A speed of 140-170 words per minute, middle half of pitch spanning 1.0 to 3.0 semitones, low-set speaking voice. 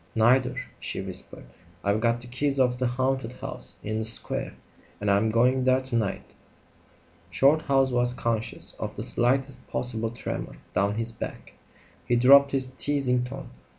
Yes: average, 155 wpm; narrow, 2.5 semitones; low, 125 Hz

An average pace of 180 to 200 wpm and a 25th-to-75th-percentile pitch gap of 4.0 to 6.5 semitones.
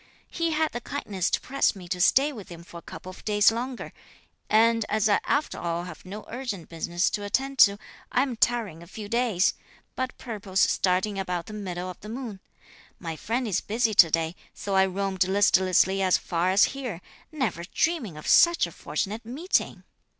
Yes: average, 195 wpm; average, 4.8 semitones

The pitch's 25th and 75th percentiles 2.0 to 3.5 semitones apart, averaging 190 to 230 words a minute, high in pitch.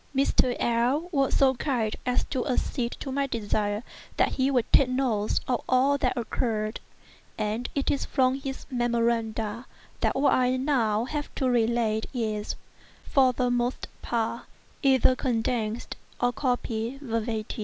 No: average, 2.8 semitones; average, 145 wpm; high, 245 Hz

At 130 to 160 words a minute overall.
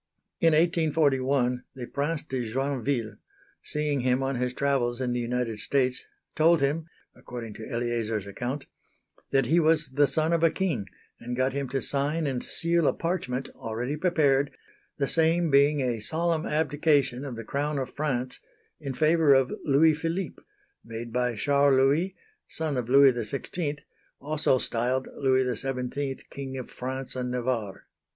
Yes: average, 155 wpm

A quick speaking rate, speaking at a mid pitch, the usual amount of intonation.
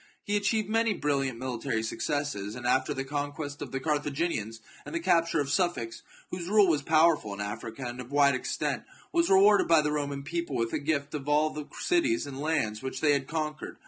Yes: fast, 210 wpm; medium, 145 Hz; average, 4.3 semitones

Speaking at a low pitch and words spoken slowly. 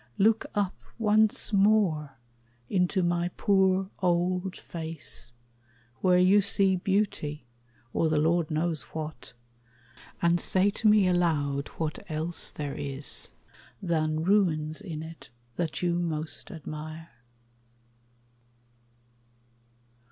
No: medium, 170 Hz; slow, 105 wpm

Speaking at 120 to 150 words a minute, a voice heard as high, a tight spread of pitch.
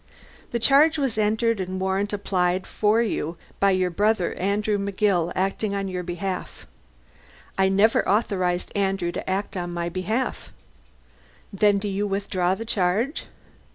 Yes: average, 140 wpm; high, 195 Hz; narrow, 2.3 semitones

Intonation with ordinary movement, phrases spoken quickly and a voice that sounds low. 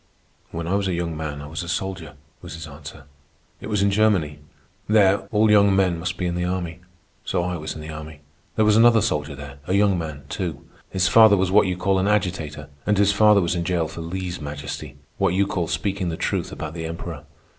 Yes: average, 3.8 semitones; fast, 225 wpm; very low, 90 Hz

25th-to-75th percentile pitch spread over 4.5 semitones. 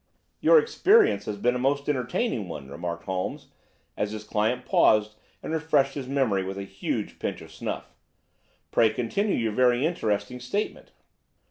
Yes: wide, 5.4 semitones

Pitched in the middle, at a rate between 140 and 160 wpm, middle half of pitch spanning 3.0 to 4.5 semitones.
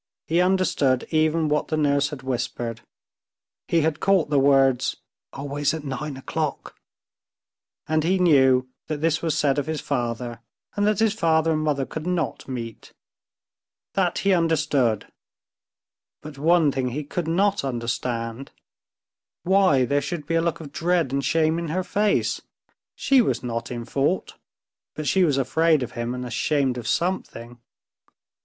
Yes: medium, 150 Hz; average, 155 wpm; average, 4.0 semitones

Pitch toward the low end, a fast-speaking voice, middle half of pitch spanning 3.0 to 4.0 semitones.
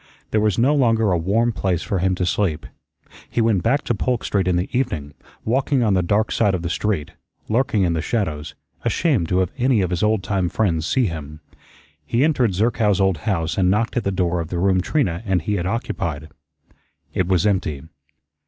No: very low, 95 Hz; fast, 210 wpm; average, 4.5 semitones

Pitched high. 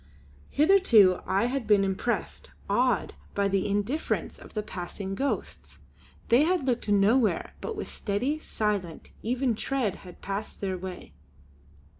Yes: high, 215 Hz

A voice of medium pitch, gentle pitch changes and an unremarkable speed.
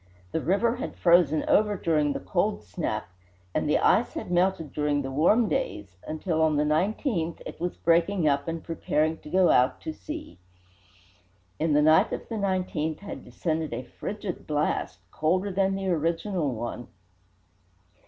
No: medium, 165 Hz; average, 4.2 semitones; average, 165 wpm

